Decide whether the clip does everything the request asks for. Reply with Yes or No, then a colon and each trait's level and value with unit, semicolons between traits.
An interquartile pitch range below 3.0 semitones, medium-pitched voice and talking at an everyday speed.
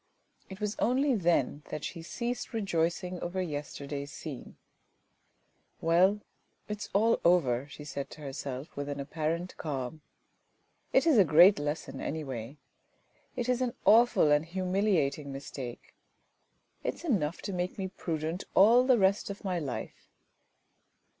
No: wide, 5.5 semitones; medium, 170 Hz; average, 145 wpm